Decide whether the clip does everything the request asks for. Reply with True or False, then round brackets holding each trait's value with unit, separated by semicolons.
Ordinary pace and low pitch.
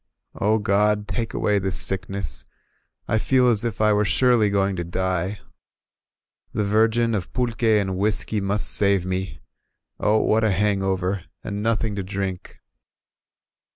True (150 wpm; 105 Hz)